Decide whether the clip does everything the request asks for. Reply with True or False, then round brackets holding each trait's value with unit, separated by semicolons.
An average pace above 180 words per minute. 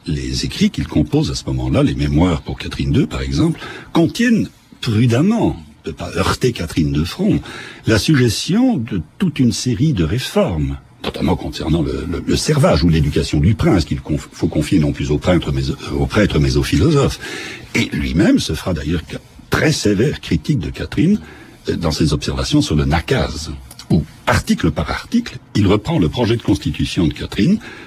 False (175 wpm)